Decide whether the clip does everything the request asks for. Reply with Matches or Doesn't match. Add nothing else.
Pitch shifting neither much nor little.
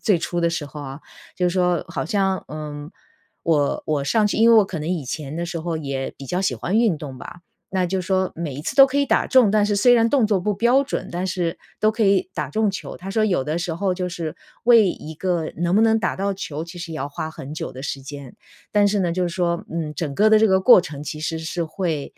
Matches